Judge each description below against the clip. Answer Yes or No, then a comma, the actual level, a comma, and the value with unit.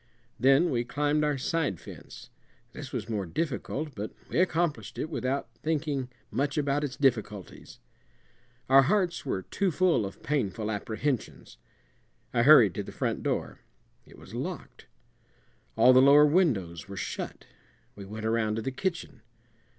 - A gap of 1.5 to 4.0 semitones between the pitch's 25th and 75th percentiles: No, wide, 5.4 semitones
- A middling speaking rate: Yes, average, 150 wpm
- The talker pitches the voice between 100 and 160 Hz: Yes, low, 135 Hz